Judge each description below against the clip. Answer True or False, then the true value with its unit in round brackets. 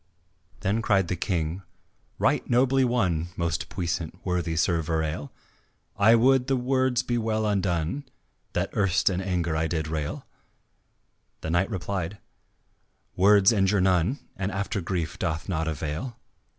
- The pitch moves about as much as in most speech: True (4.7 semitones)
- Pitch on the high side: False (95 Hz)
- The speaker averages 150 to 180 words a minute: False (135 wpm)